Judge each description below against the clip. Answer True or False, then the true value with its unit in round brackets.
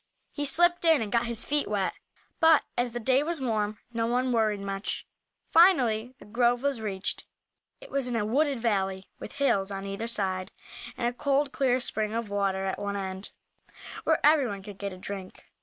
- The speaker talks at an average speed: True (190 wpm)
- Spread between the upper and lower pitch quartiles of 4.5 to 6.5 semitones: True (5.2 semitones)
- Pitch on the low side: False (230 Hz)